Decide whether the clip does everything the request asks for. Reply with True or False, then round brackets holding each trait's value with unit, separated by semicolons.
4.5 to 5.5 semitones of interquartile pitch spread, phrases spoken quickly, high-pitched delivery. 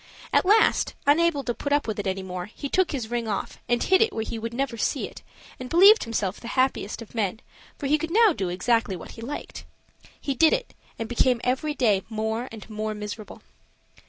True (5.2 semitones; 215 wpm; 235 Hz)